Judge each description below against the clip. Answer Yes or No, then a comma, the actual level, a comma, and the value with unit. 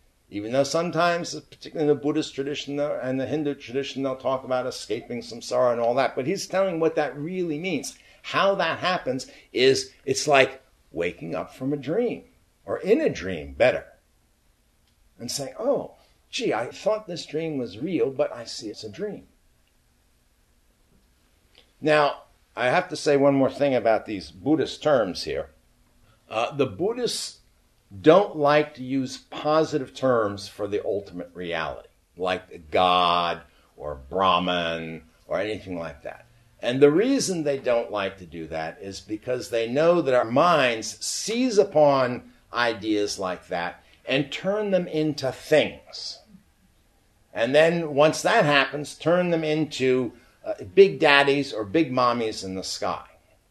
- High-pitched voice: No, low, 135 Hz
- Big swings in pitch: Yes, wide, 7.3 semitones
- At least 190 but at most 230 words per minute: No, average, 155 wpm